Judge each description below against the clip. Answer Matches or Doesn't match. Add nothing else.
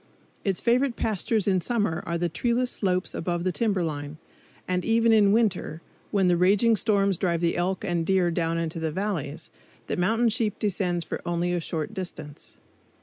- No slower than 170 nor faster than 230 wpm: Matches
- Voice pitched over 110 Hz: Matches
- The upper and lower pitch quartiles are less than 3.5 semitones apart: Doesn't match